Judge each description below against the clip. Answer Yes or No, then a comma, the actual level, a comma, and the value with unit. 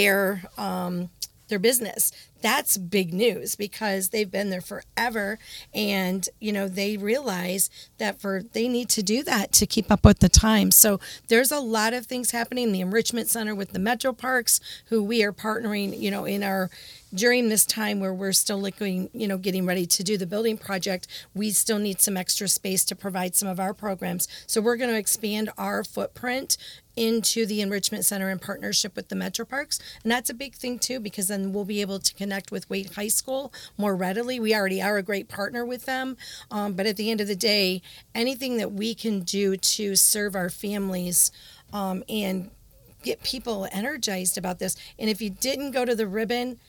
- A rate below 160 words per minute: No, average, 200 wpm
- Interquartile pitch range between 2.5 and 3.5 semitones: Yes, average, 2.8 semitones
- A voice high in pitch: Yes, high, 205 Hz